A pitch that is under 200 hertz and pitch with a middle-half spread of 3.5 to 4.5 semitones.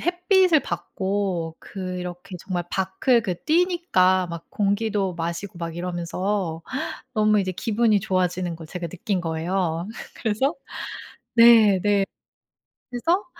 Yes: high, 190 Hz; average, 3.9 semitones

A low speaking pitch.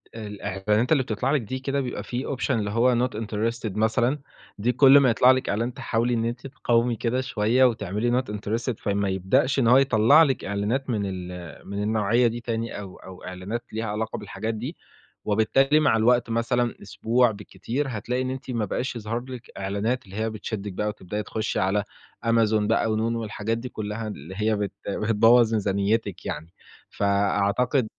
Yes: low, 115 Hz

